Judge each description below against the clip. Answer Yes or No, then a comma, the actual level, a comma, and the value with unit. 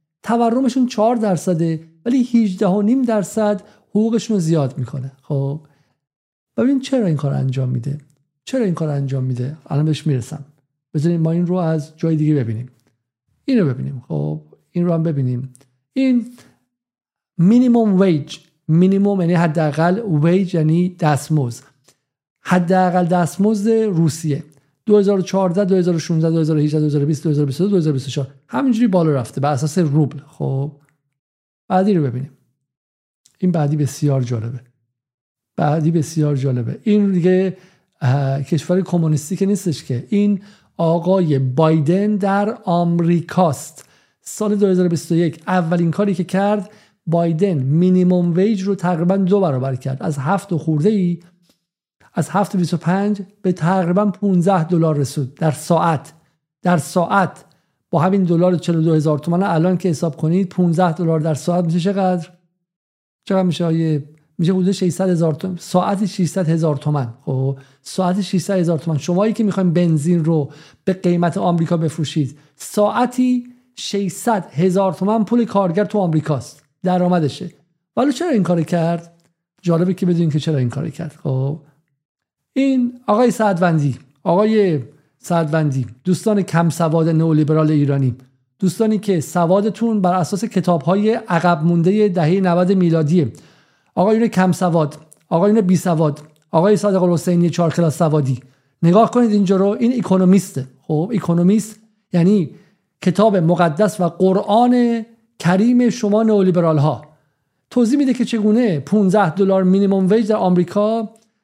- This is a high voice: No, medium, 175 Hz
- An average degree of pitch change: Yes, average, 4.5 semitones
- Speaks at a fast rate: No, average, 130 wpm